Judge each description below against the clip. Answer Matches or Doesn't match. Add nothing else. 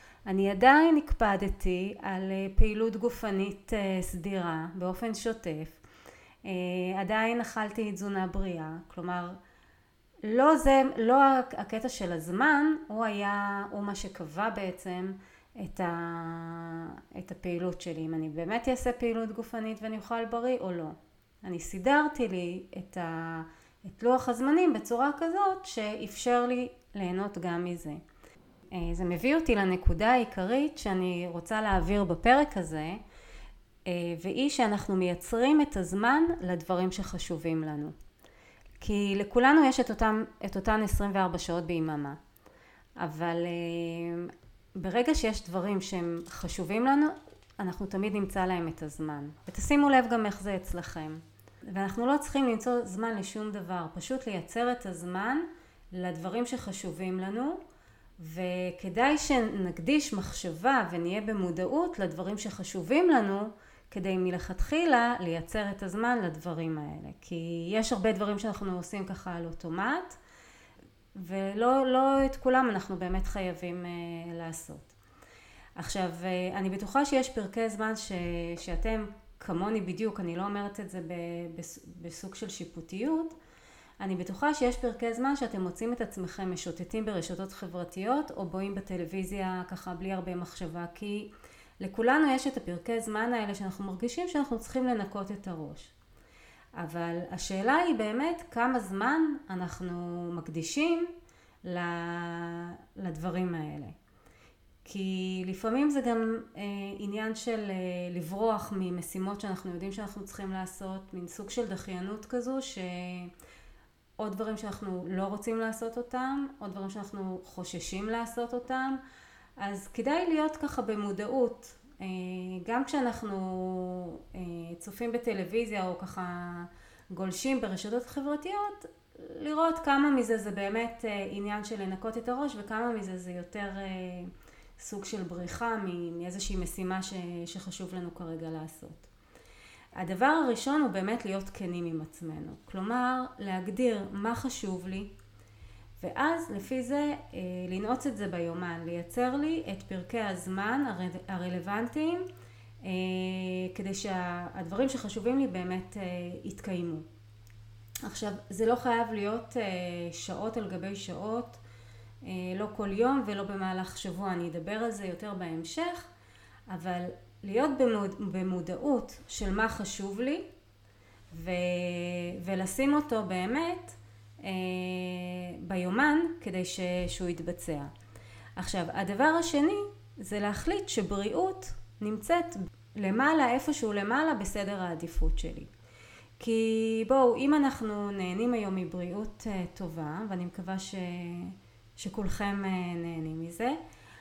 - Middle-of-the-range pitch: Doesn't match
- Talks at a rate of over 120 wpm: Doesn't match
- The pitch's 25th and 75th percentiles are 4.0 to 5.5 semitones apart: Matches